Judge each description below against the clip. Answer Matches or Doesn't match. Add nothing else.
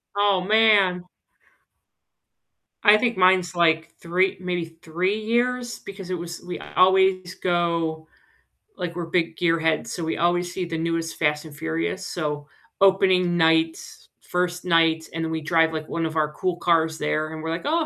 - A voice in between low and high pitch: Matches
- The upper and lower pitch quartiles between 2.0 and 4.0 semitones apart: Matches